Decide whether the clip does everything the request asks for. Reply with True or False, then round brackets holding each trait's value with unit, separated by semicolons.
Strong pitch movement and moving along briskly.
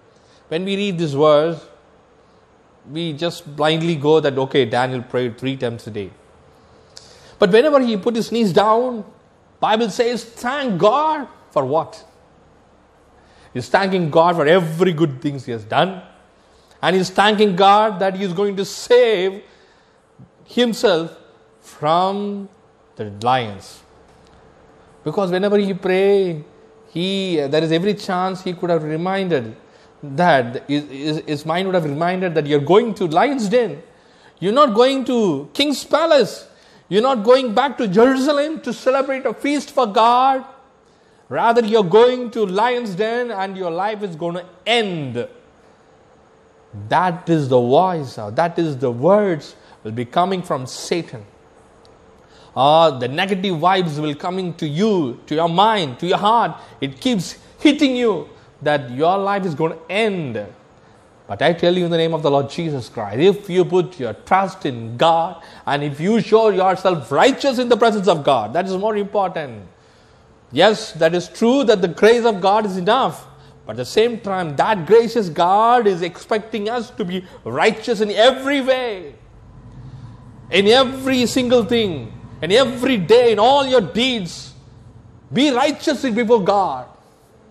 True (6.7 semitones; 160 wpm)